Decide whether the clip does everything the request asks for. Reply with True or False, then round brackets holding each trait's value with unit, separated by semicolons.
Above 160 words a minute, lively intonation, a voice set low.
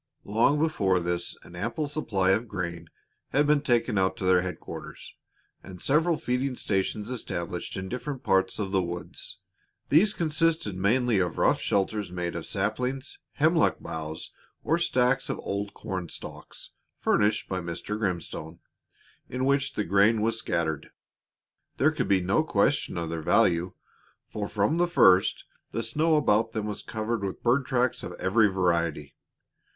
False (155 wpm; 5.7 semitones; 105 Hz)